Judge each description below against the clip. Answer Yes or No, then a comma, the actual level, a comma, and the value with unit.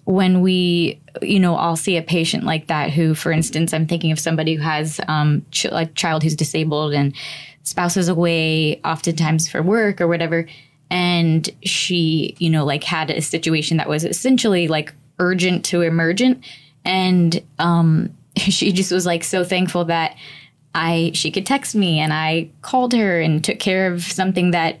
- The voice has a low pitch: No, medium, 165 Hz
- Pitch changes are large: No, narrow, 2.5 semitones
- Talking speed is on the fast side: No, average, 175 wpm